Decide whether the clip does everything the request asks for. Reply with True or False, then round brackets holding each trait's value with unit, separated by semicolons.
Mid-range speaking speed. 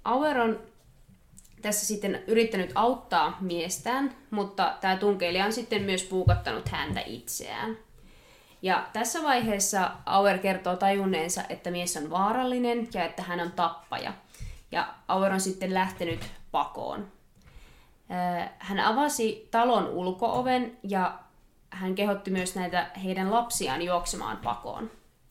True (120 wpm)